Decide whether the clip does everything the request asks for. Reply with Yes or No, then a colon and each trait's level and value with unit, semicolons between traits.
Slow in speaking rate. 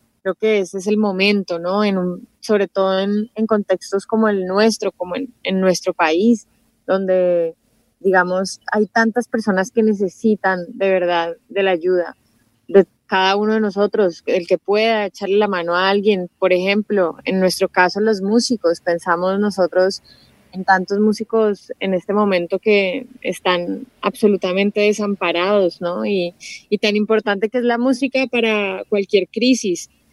No: average, 155 wpm